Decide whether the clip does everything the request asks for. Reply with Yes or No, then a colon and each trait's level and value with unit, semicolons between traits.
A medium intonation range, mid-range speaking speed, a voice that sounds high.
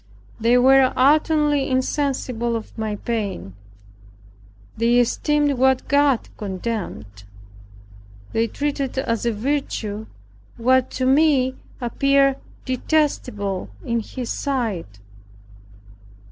No: average, 3.7 semitones; slow, 90 wpm; very high, 255 Hz